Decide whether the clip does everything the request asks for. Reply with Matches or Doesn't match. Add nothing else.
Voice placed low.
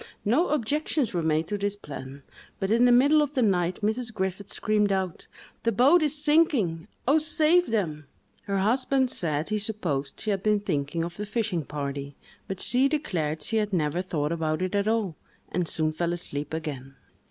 Doesn't match